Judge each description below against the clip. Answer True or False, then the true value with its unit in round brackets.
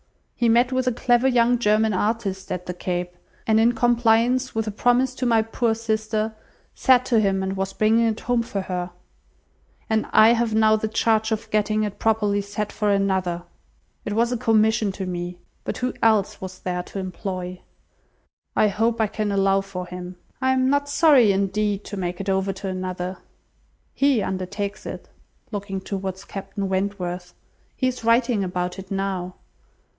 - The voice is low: False (210 Hz)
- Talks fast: False (175 wpm)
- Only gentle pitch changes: False (3.2 semitones)